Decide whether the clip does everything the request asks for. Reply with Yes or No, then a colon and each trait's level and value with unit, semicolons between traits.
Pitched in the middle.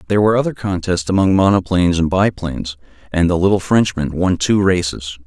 No: very low, 90 Hz